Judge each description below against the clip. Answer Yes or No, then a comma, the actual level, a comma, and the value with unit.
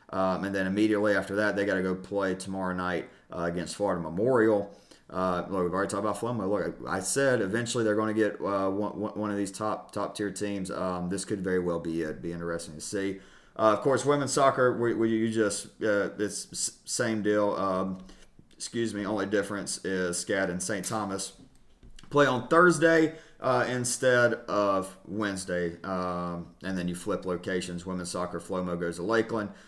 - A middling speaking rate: Yes, average, 190 wpm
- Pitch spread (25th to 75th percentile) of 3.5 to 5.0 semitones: No, average, 2.9 semitones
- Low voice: Yes, low, 100 Hz